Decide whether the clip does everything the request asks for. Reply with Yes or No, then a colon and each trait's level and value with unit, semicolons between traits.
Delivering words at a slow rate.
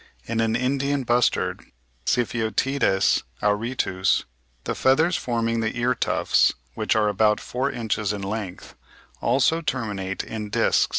Yes: slow, 125 wpm